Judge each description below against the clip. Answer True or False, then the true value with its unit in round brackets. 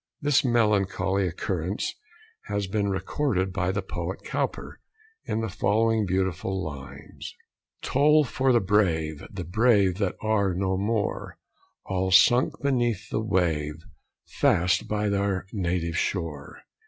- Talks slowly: True (125 wpm)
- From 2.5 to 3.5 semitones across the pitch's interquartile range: True (3.2 semitones)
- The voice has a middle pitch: False (100 Hz)